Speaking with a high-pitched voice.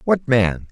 No: low, 115 Hz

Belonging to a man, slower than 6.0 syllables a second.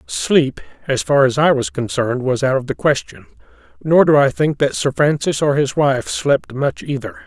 Yes: male; 4.9 syllables/s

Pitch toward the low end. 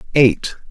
Yes: low, 125 Hz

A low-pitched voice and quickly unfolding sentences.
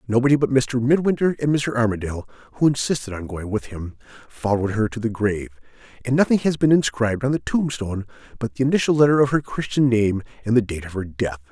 Yes: low, 120 Hz; fast, 210 wpm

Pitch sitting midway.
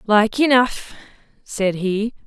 No: high, 220 Hz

